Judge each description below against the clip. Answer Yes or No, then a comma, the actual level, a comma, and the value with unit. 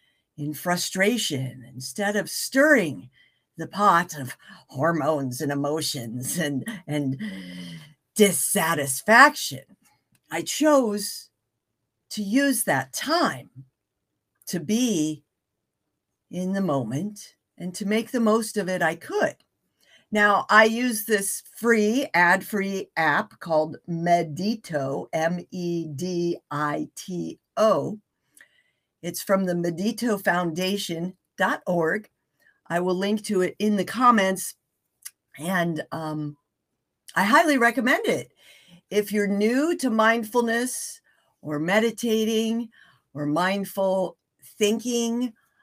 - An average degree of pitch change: No, wide, 6.5 semitones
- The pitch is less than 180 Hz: No, medium, 185 Hz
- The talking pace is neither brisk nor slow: No, slow, 105 wpm